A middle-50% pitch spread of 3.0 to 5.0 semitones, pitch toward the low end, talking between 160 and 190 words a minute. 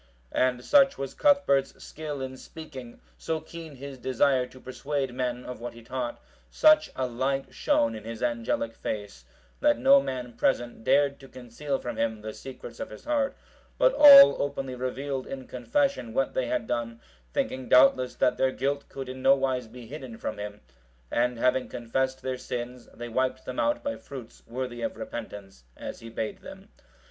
No: narrow, 2.5 semitones; low, 130 Hz; average, 175 wpm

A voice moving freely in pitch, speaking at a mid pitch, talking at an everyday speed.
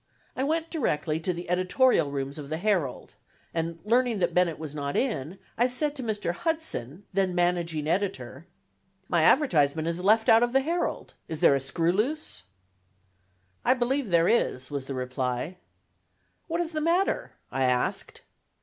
Yes: wide, 8.6 semitones; medium, 180 Hz; average, 165 wpm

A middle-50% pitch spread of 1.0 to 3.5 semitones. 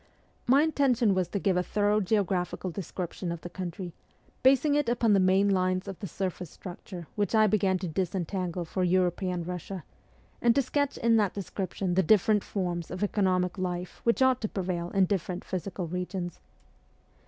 Yes: average, 2.7 semitones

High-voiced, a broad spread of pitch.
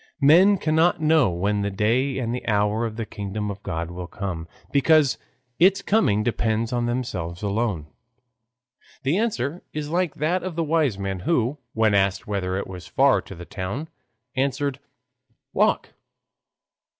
No: low, 115 Hz; wide, 7.2 semitones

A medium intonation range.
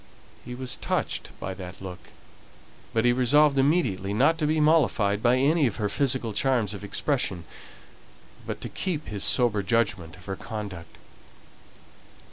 No: wide, 5.7 semitones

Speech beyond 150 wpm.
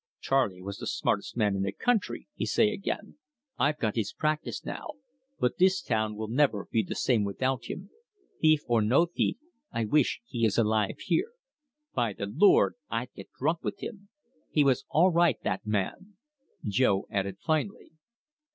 Yes: average, 170 wpm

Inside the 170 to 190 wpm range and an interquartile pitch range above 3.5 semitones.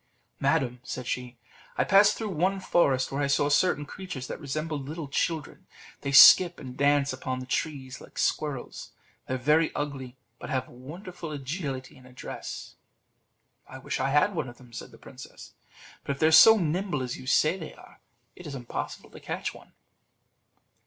Yes: average, 180 wpm; average, 3.9 semitones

